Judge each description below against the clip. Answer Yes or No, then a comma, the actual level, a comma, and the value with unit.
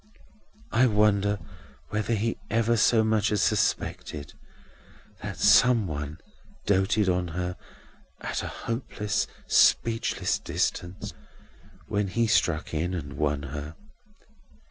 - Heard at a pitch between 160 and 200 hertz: No, low, 100 Hz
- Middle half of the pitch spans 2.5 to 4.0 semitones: No, average, 4.6 semitones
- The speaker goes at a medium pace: No, slow, 110 wpm